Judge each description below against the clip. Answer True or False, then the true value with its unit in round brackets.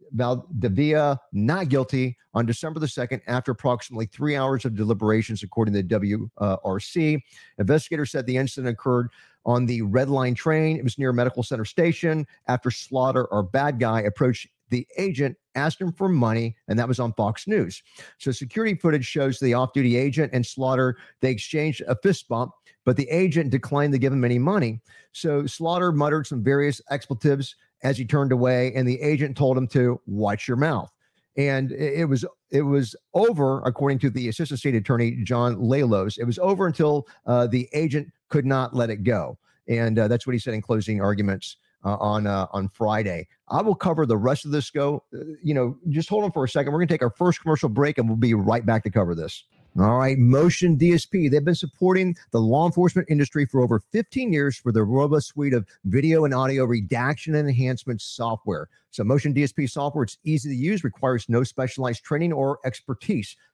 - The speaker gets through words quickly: False (195 wpm)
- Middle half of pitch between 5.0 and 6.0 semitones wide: False (3.9 semitones)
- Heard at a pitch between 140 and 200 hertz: False (130 Hz)